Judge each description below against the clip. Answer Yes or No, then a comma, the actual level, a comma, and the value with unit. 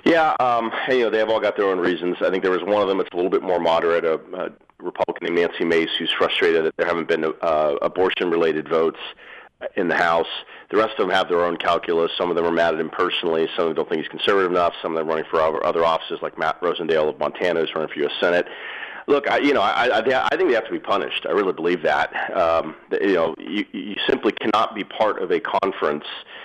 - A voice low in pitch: Yes, low, 110 Hz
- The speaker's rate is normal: No, fast, 260 wpm